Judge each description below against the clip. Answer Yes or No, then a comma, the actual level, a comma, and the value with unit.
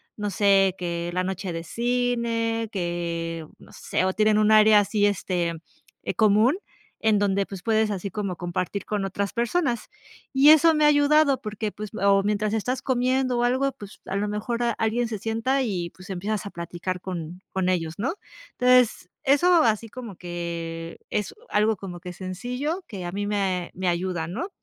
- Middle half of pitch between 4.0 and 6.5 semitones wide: Yes, average, 4.5 semitones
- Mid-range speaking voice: No, high, 205 Hz